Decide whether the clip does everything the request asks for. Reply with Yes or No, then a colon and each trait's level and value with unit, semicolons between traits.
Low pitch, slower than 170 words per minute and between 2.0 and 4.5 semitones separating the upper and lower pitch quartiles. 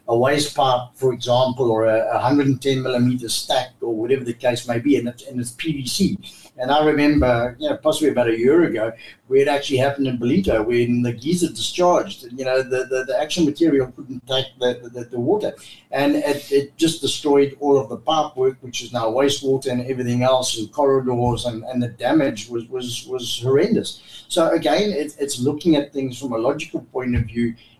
No: low, 130 Hz; fast, 205 wpm; average, 2.8 semitones